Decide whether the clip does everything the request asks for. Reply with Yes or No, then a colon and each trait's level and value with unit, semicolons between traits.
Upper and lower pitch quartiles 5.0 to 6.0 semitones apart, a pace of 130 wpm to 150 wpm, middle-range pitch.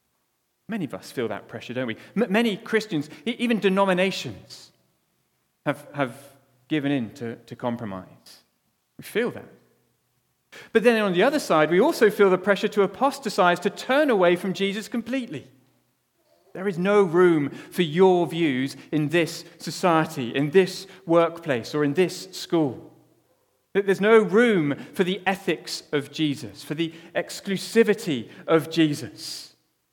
Yes: average, 5.3 semitones; average, 140 wpm; medium, 175 Hz